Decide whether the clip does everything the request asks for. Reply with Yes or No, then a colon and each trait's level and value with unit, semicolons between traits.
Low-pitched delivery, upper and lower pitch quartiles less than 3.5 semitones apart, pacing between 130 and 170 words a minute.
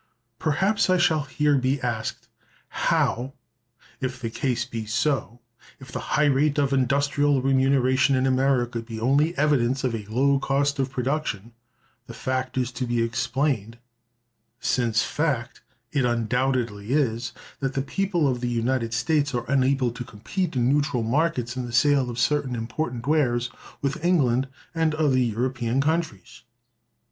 Yes: low, 130 Hz; average, 3.0 semitones; average, 145 wpm